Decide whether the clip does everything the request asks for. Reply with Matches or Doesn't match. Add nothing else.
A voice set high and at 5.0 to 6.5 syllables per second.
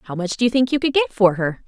Matches